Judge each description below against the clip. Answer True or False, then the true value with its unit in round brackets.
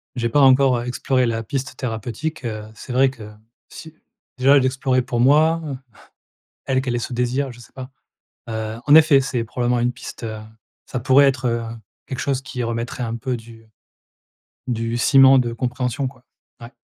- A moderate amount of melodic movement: False (2.3 semitones)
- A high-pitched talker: False (125 Hz)